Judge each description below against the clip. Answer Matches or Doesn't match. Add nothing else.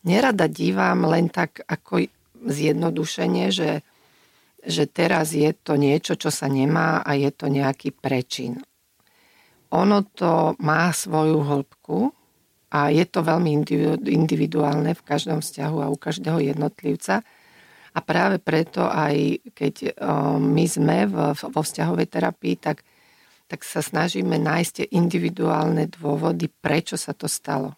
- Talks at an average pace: Matches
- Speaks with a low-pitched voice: Doesn't match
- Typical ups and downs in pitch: Doesn't match